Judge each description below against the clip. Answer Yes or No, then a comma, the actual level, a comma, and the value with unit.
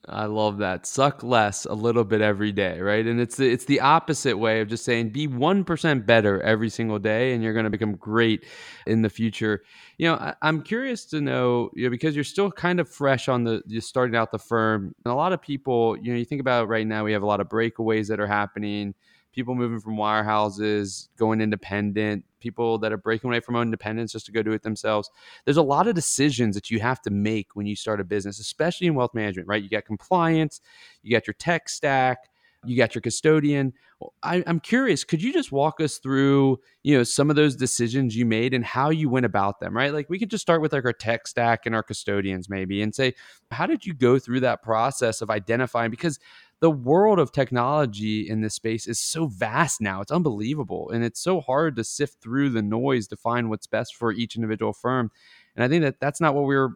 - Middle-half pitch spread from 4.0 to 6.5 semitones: Yes, average, 4.5 semitones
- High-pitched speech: No, low, 115 Hz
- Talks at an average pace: No, fast, 230 wpm